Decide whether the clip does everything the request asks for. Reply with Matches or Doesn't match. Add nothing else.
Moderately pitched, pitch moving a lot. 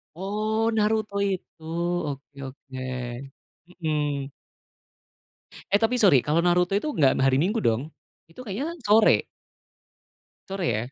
Matches